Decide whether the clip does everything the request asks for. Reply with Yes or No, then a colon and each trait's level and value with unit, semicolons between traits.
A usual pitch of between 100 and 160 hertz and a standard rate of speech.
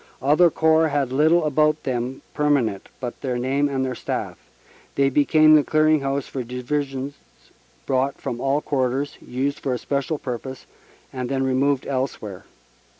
Yes: low, 135 Hz; average, 155 wpm